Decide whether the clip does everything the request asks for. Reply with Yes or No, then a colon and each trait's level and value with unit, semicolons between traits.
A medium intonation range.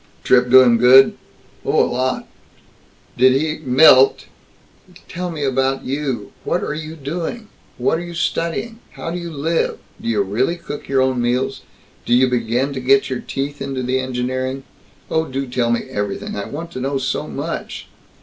Yes: average, 3.4 semitones